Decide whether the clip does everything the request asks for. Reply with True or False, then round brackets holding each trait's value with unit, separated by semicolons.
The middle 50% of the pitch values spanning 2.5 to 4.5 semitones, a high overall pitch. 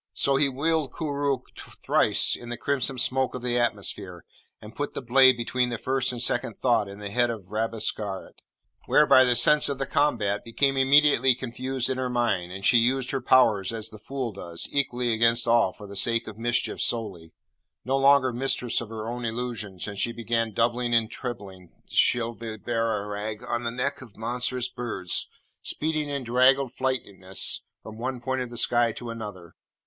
False (3.0 semitones; 120 Hz)